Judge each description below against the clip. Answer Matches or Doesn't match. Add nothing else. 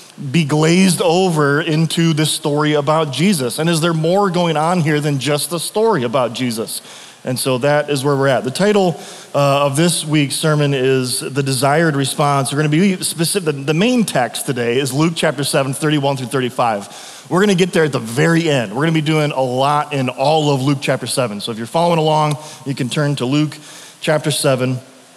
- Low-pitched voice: Doesn't match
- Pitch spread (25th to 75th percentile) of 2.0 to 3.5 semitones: Matches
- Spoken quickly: Matches